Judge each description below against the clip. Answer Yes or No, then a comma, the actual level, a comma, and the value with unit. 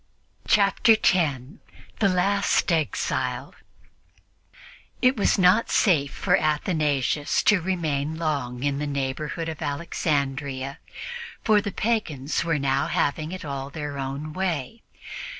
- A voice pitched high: No, medium, 155 Hz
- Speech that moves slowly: Yes, slow, 115 wpm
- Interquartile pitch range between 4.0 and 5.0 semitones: Yes, average, 4.7 semitones